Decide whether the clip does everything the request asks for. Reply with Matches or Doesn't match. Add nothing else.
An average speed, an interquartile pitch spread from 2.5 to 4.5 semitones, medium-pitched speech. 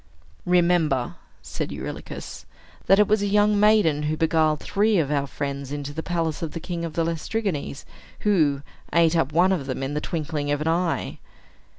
Matches